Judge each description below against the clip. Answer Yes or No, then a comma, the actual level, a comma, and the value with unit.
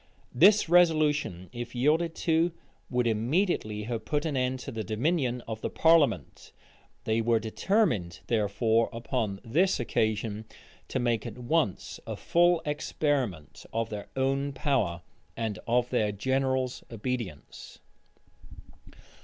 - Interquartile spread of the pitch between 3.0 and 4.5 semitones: No, average, 5.1 semitones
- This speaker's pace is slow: Yes, slow, 125 wpm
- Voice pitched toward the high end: No, low, 125 Hz